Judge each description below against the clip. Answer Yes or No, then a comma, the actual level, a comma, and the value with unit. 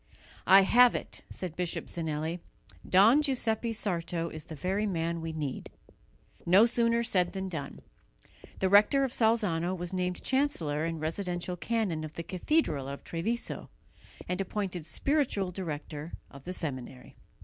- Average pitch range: Yes, average, 4.8 semitones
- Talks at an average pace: Yes, average, 145 wpm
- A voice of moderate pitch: Yes, medium, 180 Hz